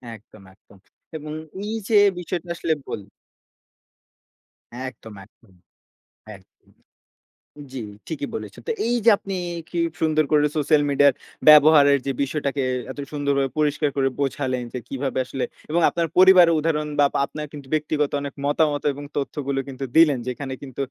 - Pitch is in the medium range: Yes, medium, 145 Hz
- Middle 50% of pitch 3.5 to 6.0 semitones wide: No, narrow, 2.4 semitones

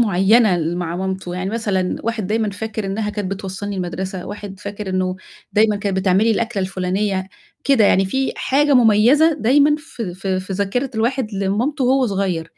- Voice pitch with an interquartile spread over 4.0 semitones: No, average, 3.3 semitones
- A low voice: No, high, 205 Hz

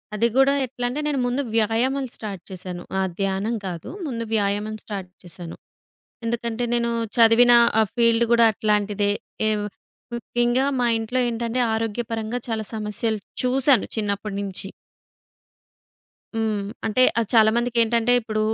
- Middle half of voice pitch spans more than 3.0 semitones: No, narrow, 2.4 semitones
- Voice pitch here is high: Yes, high, 225 Hz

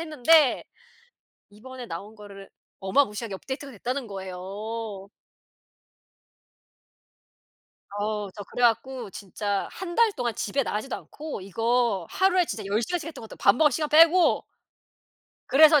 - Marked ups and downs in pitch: Yes, wide, 6.4 semitones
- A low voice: No, high, 235 Hz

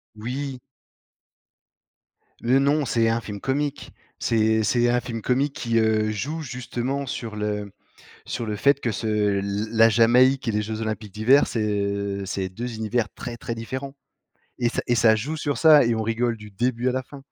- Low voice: Yes, low, 115 Hz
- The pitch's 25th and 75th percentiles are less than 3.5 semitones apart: Yes, average, 3.1 semitones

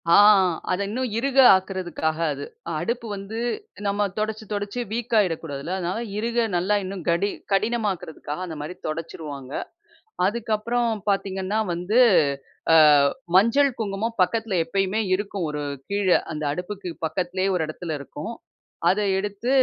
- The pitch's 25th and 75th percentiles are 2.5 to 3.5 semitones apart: No, average, 4.0 semitones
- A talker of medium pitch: No, high, 195 Hz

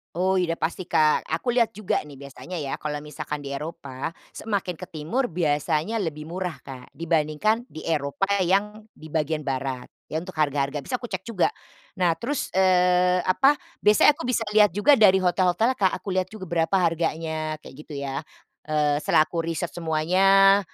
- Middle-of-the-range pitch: Yes, medium, 170 Hz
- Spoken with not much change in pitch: No, average, 4.2 semitones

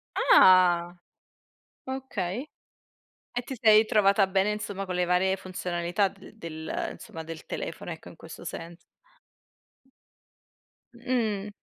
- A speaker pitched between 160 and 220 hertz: Yes, high, 190 Hz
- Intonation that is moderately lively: Yes, average, 3.2 semitones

